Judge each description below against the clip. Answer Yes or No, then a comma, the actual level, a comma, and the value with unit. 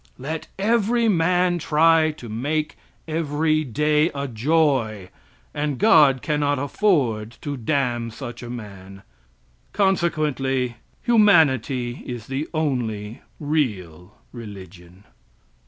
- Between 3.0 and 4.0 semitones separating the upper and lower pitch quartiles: No, wide, 5.4 semitones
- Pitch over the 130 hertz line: Yes, medium, 140 Hz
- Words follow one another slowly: Yes, slow, 100 wpm